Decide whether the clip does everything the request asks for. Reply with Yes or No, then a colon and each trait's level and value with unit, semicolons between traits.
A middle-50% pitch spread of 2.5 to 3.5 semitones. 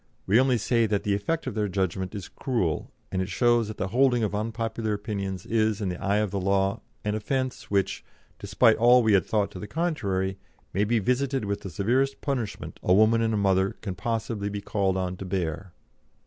Yes: average, 3.1 semitones